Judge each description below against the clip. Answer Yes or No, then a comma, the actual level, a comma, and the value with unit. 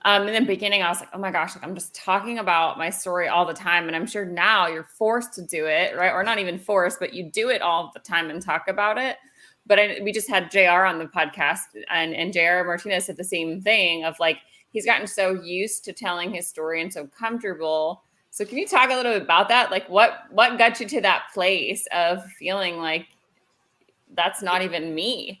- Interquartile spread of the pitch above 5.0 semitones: No, average, 3.4 semitones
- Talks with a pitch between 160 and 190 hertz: Yes, medium, 185 Hz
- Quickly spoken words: Yes, fast, 235 wpm